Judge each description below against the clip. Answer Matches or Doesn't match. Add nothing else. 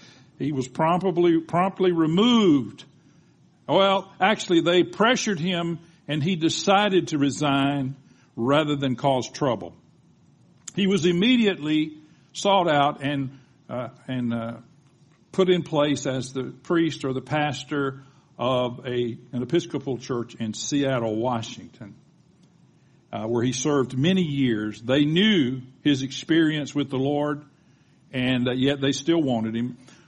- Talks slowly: Matches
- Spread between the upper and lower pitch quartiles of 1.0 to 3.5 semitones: Doesn't match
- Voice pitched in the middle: Matches